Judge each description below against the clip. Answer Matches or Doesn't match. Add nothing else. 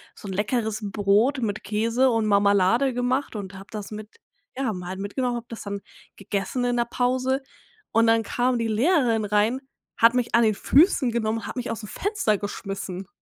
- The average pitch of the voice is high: Matches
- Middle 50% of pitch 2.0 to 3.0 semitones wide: Doesn't match